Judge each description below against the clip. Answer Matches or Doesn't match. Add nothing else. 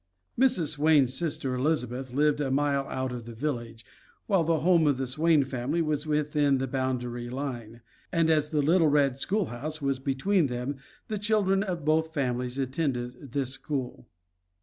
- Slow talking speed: Doesn't match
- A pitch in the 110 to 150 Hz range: Matches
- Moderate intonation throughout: Matches